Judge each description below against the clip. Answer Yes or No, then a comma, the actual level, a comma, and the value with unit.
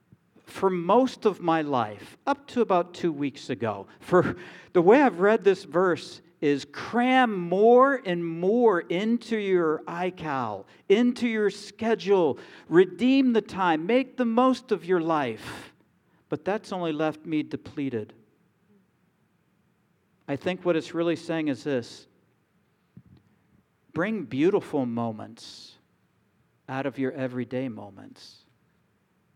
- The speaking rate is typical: No, slow, 125 wpm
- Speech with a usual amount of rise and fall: No, wide, 6.4 semitones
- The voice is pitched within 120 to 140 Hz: No, medium, 175 Hz